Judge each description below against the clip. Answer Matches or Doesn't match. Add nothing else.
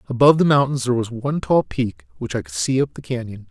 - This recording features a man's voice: Matches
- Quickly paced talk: Matches